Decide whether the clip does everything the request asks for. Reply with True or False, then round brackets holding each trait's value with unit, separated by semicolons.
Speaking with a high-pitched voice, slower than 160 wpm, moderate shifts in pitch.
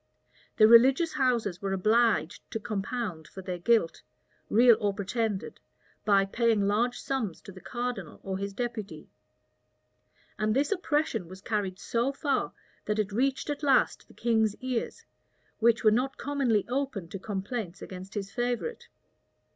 True (220 Hz; 145 wpm; 4.1 semitones)